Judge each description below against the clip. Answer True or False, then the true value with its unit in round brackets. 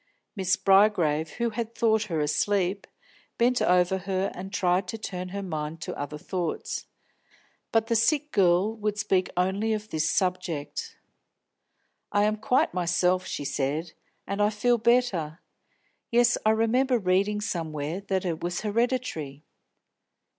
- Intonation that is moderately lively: True (4.0 semitones)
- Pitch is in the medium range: False (195 Hz)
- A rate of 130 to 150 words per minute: True (140 wpm)